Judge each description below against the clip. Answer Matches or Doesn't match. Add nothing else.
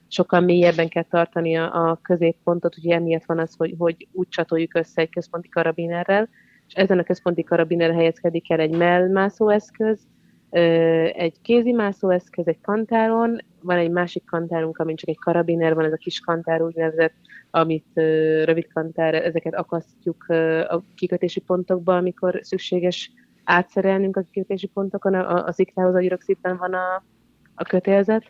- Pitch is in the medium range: Matches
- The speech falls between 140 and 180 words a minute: Matches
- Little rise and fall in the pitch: Matches